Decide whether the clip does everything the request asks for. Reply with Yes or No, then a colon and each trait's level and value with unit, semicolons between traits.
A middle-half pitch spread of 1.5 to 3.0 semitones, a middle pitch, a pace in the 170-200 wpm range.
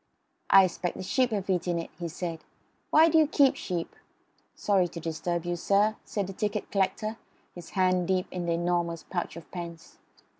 Yes: average, 2.7 semitones; medium, 180 Hz; average, 185 wpm